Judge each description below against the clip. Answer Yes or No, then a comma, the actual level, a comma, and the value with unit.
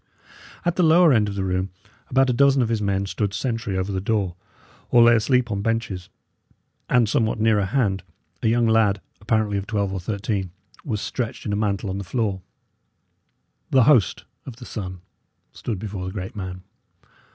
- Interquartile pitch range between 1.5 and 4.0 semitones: Yes, average, 3.3 semitones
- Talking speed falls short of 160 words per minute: No, average, 185 wpm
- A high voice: No, low, 105 Hz